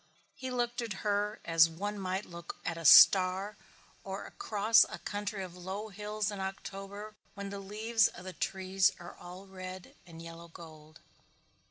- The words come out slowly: No, average, 165 wpm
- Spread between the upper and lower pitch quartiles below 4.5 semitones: Yes, narrow, 2.6 semitones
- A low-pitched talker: No, high, 195 Hz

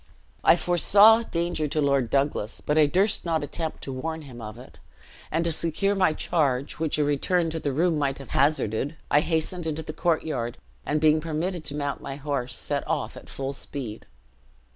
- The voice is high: No, medium, 150 Hz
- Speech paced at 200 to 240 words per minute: No, average, 190 wpm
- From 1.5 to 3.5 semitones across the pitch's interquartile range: Yes, average, 3.2 semitones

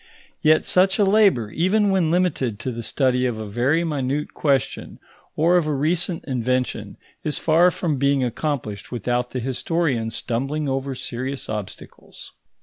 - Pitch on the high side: No, medium, 140 Hz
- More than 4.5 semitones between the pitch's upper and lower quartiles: Yes, average, 5.0 semitones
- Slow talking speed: No, average, 150 wpm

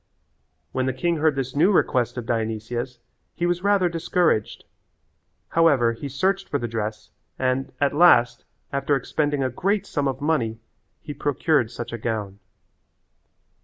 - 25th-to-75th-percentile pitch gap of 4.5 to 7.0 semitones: Yes, average, 5.3 semitones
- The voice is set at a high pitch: No, low, 135 Hz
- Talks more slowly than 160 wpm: Yes, average, 150 wpm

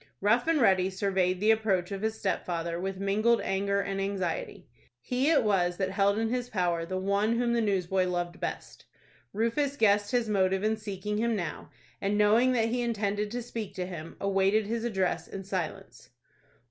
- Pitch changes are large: No, average, 2.9 semitones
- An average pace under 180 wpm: No, average, 185 wpm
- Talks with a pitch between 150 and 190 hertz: No, high, 200 Hz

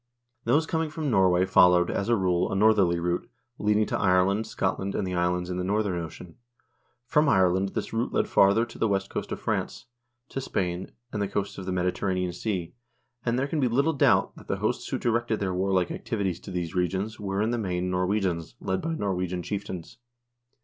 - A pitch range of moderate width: Yes, average, 3.4 semitones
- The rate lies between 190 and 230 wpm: Yes, average, 200 wpm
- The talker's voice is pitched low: Yes, very low, 95 Hz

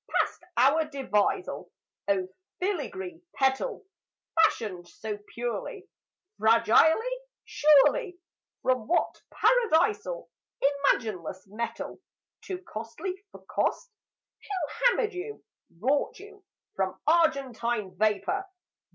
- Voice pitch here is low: No, very high, 290 Hz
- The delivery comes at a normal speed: No, slow, 90 wpm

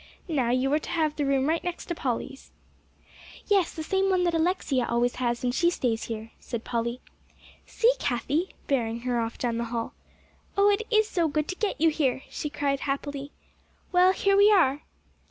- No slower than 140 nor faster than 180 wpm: No, average, 190 wpm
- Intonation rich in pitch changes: Yes, wide, 6.4 semitones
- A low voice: No, very high, 285 Hz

